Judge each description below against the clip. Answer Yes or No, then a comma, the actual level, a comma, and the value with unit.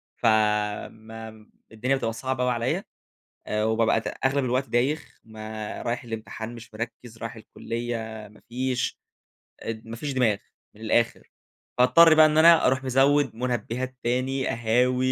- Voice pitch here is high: No, low, 120 Hz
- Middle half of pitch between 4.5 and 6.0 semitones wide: No, narrow, 2.6 semitones